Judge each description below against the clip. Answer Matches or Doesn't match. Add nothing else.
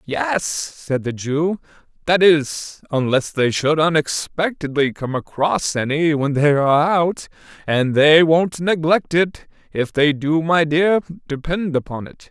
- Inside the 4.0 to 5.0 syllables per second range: Doesn't match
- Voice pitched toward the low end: Doesn't match